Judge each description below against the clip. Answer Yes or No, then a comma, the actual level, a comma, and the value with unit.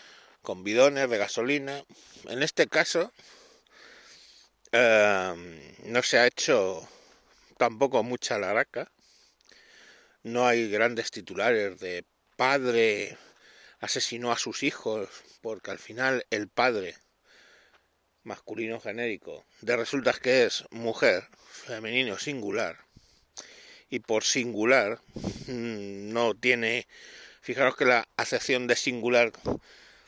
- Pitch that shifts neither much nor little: No, narrow, 1.7 semitones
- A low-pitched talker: Yes, low, 120 Hz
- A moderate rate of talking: No, slow, 100 wpm